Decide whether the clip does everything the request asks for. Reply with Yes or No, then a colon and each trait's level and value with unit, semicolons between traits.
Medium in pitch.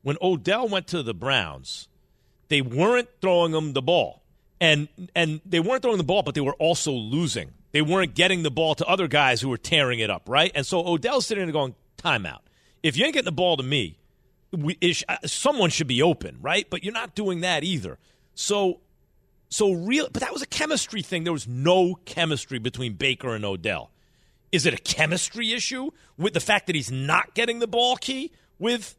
Yes: medium, 170 Hz